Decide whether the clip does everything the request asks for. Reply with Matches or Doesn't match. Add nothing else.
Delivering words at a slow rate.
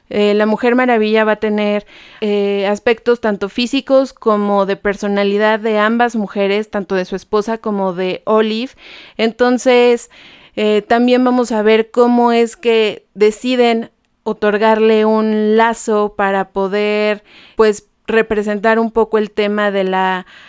Doesn't match